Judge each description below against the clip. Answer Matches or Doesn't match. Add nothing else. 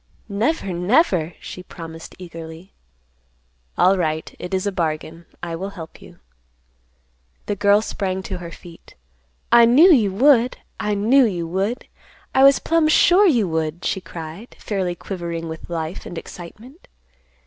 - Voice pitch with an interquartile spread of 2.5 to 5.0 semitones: Doesn't match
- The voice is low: Doesn't match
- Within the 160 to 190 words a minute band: Doesn't match